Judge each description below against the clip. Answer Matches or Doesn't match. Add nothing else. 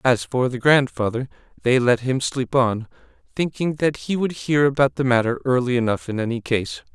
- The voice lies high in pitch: Doesn't match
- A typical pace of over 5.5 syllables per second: Doesn't match